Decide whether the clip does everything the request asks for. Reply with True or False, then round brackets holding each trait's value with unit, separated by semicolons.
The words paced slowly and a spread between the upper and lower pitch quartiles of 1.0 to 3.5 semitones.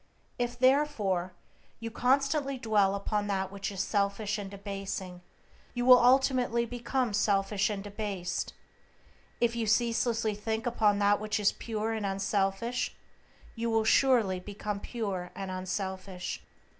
True (130 wpm; 3.2 semitones)